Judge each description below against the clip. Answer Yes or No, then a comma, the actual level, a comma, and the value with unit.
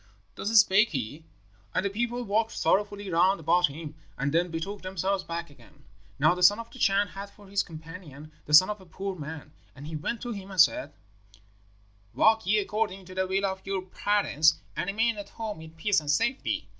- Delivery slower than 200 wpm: No, fast, 205 wpm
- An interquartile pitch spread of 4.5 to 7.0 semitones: No, average, 4.1 semitones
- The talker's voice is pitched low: No, high, 190 Hz